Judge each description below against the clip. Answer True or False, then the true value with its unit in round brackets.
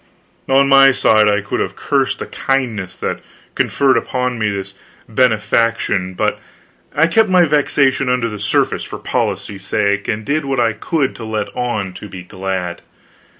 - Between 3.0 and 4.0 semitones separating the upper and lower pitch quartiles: False (5.0 semitones)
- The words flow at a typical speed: True (165 wpm)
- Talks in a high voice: False (115 Hz)